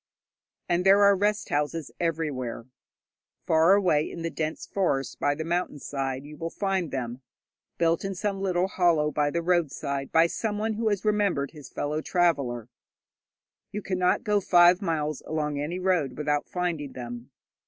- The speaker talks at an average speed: Yes, average, 155 wpm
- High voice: No, medium, 165 Hz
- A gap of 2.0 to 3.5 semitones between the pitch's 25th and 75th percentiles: No, average, 4.1 semitones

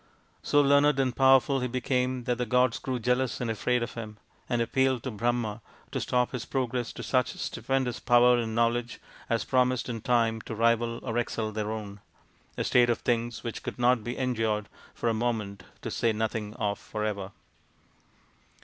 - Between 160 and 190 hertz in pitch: No, low, 120 Hz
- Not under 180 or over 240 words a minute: Yes, average, 185 wpm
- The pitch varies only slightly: Yes, narrow, 2.1 semitones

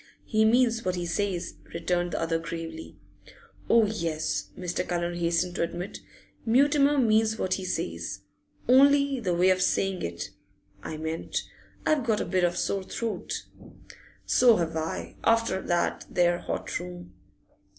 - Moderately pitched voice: Yes, medium, 180 Hz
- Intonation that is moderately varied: Yes, average, 4.9 semitones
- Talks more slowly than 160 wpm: Yes, average, 150 wpm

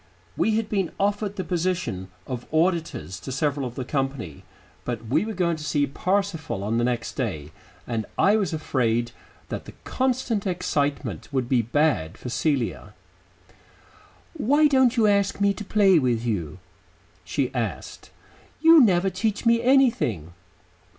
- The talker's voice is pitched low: No, medium, 155 Hz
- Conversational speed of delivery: Yes, average, 150 wpm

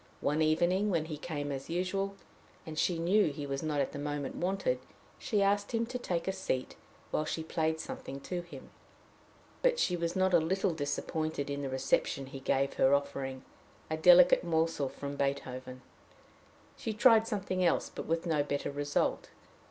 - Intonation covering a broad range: No, average, 4.7 semitones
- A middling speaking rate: Yes, average, 175 wpm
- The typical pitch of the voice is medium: Yes, medium, 160 Hz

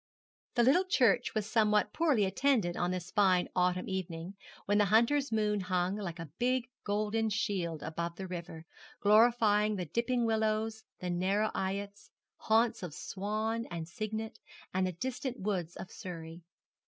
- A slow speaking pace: No, average, 155 wpm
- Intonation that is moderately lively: Yes, average, 3.7 semitones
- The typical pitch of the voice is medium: No, high, 205 Hz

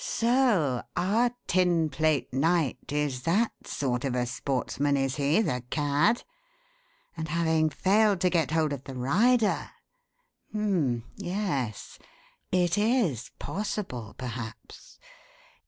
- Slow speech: Yes, slow, 110 wpm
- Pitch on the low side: No, medium, 155 Hz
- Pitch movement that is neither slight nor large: No, wide, 6.7 semitones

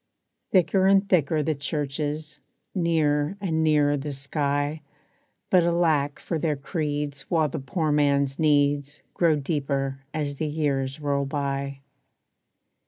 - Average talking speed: No, slow, 120 wpm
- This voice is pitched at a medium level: Yes, medium, 145 Hz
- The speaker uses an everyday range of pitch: No, narrow, 2.2 semitones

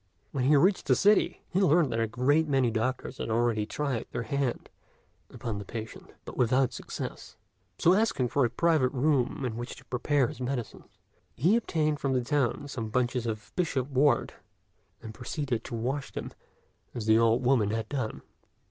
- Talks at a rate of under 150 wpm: No, average, 180 wpm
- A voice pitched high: No, low, 130 Hz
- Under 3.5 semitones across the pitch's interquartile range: No, average, 3.8 semitones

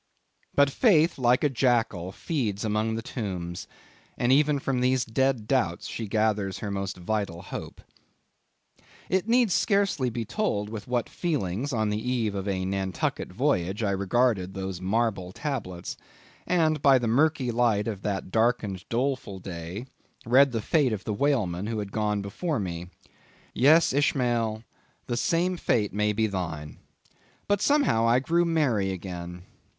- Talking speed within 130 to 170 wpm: Yes, average, 155 wpm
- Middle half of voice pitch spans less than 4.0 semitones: No, wide, 5.4 semitones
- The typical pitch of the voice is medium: No, low, 110 Hz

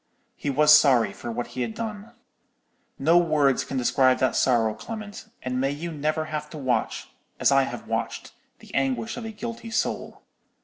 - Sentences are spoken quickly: No, average, 180 wpm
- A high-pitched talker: No, medium, 145 Hz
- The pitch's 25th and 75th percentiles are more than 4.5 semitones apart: Yes, average, 5.1 semitones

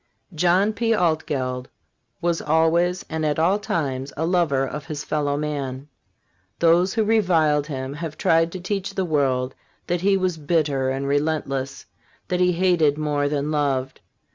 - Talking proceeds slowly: No, average, 155 wpm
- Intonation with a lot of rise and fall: No, average, 3.8 semitones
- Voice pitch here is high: No, medium, 155 Hz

